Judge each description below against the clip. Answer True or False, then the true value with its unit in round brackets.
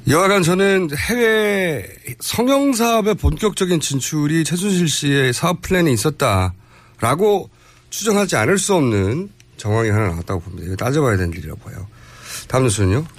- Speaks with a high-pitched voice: False (145 Hz)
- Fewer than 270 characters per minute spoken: False (340 characters per minute)